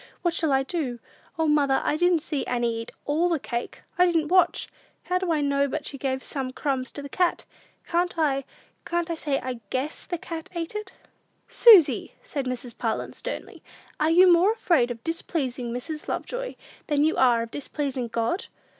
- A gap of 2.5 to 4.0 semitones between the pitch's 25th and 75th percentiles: No, average, 4.8 semitones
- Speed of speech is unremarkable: Yes, average, 190 wpm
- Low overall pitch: No, very high, 295 Hz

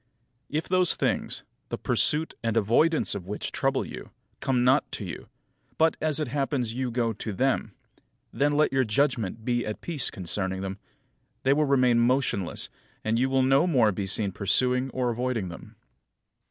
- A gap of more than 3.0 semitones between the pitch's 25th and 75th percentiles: Yes, average, 4.3 semitones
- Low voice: Yes, low, 125 Hz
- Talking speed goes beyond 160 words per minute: Yes, average, 175 wpm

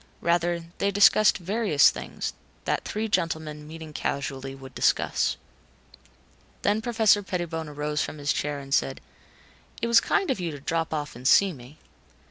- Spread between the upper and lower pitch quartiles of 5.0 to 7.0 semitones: Yes, wide, 5.5 semitones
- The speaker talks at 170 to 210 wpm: No, average, 155 wpm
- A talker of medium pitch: Yes, medium, 160 Hz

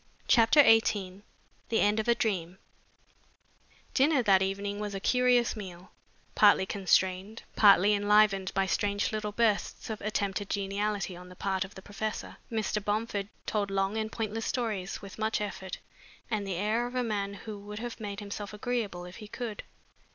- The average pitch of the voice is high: Yes, high, 205 Hz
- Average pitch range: No, narrow, 2.0 semitones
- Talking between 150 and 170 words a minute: Yes, average, 165 wpm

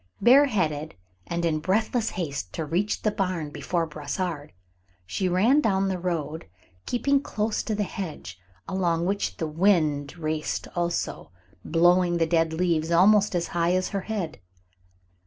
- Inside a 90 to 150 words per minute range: Yes, average, 145 wpm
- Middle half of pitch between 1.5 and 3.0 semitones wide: No, average, 3.8 semitones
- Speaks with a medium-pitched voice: Yes, medium, 175 Hz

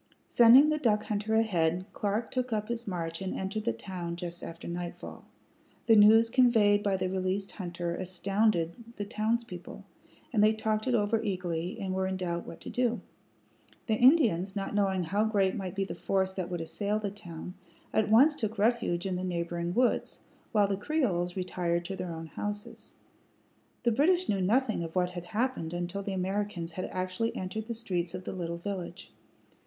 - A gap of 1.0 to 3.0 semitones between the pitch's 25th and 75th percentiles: No, average, 3.7 semitones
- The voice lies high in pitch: Yes, high, 195 Hz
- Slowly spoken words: No, average, 185 wpm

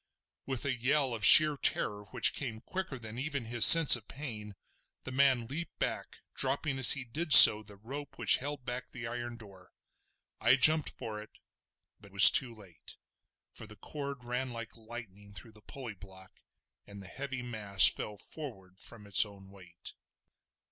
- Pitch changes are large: No, average, 4.6 semitones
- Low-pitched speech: Yes, low, 120 Hz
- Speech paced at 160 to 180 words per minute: Yes, average, 175 wpm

